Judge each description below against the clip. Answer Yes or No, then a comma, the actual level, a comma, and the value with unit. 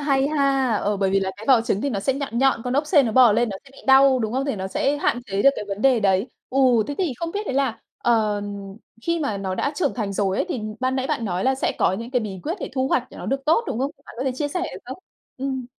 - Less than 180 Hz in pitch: No, very high, 255 Hz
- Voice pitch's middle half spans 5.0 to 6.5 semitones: No, average, 4.6 semitones